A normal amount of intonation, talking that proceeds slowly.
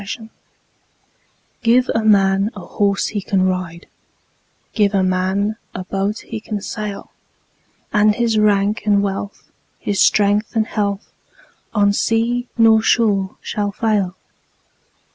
No: narrow, 1.8 semitones; slow, 125 wpm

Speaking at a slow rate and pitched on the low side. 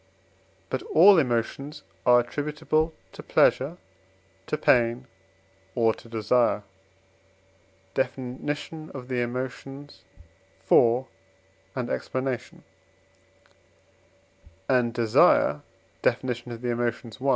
Yes: slow, 85 wpm; low, 125 Hz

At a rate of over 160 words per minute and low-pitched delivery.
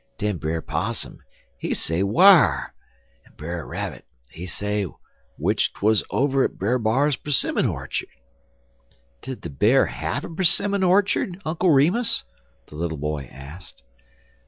No: slow, 135 wpm; low, 110 Hz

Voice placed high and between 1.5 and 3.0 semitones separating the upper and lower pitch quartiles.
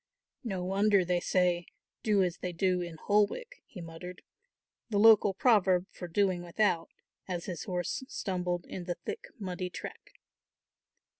No: medium, 180 Hz; narrow, 2.4 semitones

